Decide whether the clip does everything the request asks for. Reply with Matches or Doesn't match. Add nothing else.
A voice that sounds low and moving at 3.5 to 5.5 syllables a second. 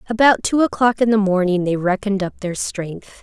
Doesn't match